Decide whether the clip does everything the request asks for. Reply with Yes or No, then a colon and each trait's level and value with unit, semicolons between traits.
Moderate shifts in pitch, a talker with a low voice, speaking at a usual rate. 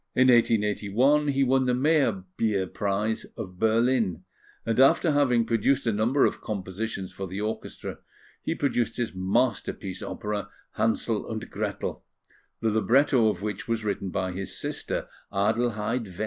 Yes: average, 4.0 semitones; low, 110 Hz; average, 145 wpm